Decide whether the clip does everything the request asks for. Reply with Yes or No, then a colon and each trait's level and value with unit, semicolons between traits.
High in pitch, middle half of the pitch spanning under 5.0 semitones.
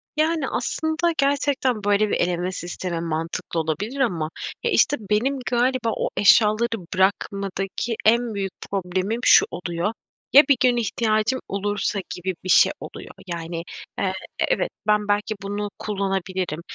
Yes: high, 205 Hz; average, 4.4 semitones